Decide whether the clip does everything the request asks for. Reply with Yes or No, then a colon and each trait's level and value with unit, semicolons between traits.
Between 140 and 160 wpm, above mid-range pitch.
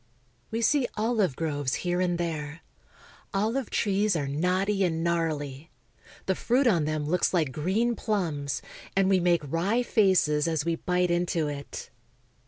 No: average, 150 wpm; medium, 175 Hz